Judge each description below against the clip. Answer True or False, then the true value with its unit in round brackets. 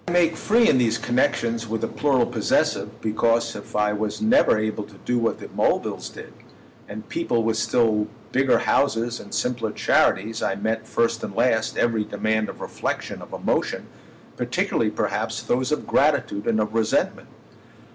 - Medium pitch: False (115 Hz)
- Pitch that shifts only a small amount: True (2.3 semitones)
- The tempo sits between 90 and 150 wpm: False (165 wpm)